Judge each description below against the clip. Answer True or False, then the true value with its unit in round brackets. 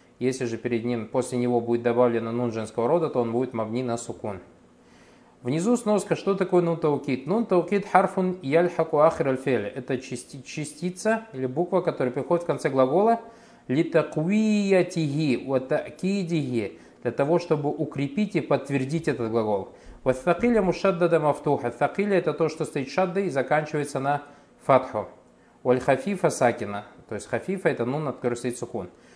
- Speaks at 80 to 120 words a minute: False (135 wpm)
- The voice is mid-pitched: True (145 Hz)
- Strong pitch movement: True (6.1 semitones)